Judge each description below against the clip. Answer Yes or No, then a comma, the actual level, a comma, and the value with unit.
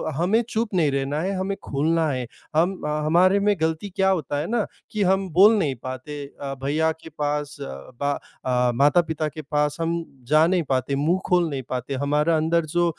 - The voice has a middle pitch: Yes, medium, 155 Hz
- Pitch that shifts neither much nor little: Yes, average, 3.7 semitones